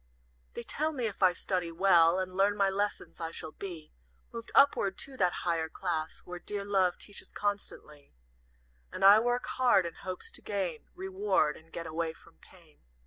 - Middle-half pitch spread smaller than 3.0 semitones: No, average, 3.6 semitones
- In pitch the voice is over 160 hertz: Yes, medium, 185 Hz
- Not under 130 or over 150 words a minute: No, average, 180 wpm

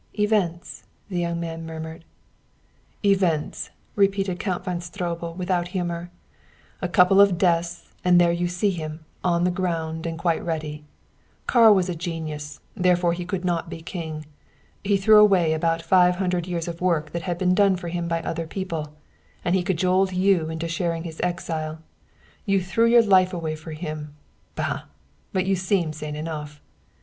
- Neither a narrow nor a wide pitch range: No, narrow, 2.2 semitones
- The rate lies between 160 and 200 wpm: Yes, average, 170 wpm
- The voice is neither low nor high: Yes, medium, 175 Hz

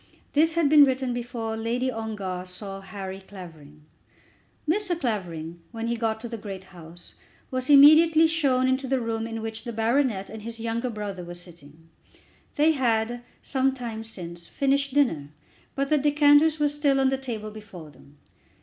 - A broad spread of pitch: Yes, wide, 5.8 semitones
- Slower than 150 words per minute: No, average, 170 wpm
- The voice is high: Yes, high, 230 Hz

